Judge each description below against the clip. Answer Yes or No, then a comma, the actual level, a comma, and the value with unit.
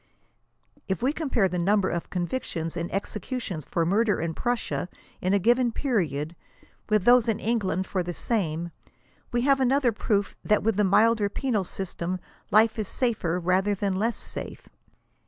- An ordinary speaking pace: Yes, average, 160 wpm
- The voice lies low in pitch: No, high, 205 Hz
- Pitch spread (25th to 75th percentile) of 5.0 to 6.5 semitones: No, average, 4.5 semitones